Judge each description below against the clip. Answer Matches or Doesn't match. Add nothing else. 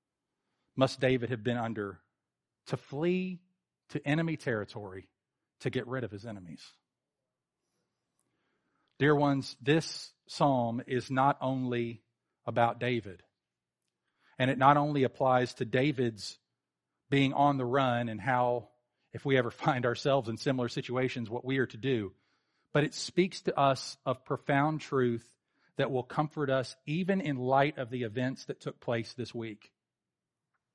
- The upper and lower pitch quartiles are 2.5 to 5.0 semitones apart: Matches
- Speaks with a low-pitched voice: Matches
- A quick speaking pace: Doesn't match